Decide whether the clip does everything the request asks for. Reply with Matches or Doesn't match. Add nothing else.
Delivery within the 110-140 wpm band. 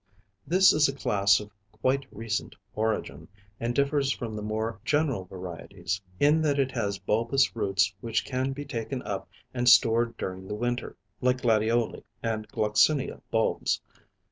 Doesn't match